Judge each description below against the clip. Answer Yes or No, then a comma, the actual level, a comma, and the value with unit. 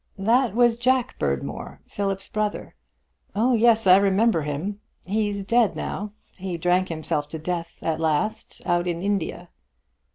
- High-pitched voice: Yes, high, 195 Hz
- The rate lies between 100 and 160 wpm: Yes, average, 140 wpm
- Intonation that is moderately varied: Yes, average, 4.2 semitones